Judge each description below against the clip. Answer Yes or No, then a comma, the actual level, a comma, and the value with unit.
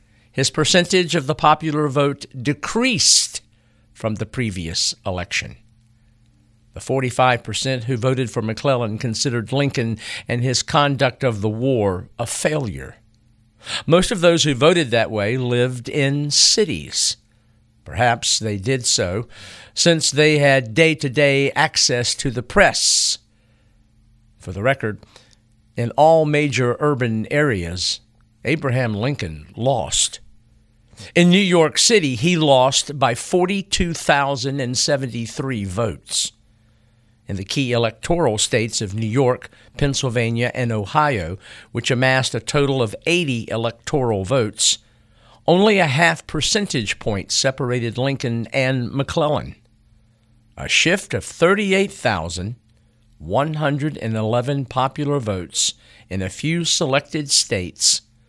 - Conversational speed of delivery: No, slow, 115 wpm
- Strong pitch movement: No, average, 4.0 semitones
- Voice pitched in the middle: No, low, 120 Hz